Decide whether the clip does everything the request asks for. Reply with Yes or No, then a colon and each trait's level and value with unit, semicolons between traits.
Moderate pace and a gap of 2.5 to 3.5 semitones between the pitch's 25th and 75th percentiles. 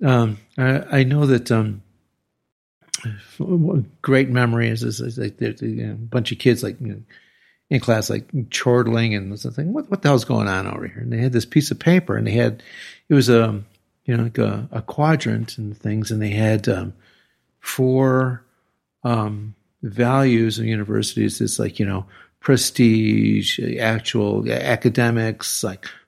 Yes: average, 170 wpm; average, 3.0 semitones